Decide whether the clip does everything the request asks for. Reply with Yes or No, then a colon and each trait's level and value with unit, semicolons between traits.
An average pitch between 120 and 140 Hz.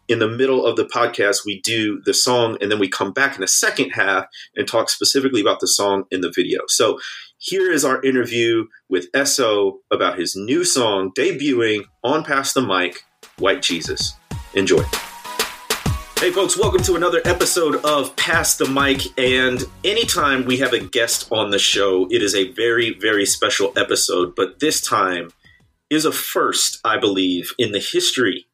Yes: low, 135 Hz